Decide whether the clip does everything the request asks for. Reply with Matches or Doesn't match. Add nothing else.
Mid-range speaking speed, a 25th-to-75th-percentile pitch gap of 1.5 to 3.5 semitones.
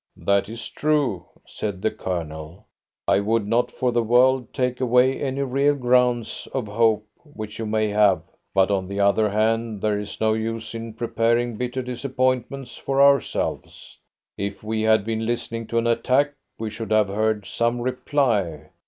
Matches